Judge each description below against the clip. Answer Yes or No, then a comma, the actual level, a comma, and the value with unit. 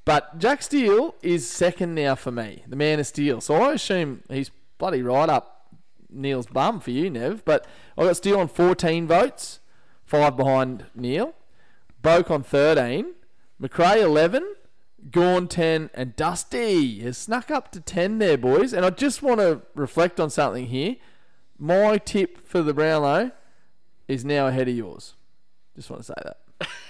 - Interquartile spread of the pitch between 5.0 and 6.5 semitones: Yes, wide, 5.5 semitones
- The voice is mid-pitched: Yes, medium, 160 Hz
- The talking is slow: No, average, 160 wpm